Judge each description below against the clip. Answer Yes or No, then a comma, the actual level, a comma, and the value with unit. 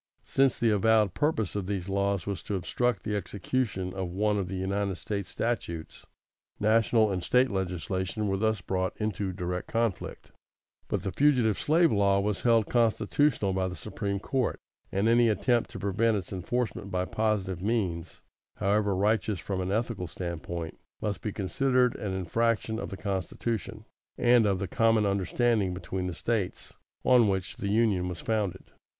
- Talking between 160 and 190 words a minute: Yes, average, 165 wpm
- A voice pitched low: Yes, low, 100 Hz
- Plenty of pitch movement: No, average, 3.3 semitones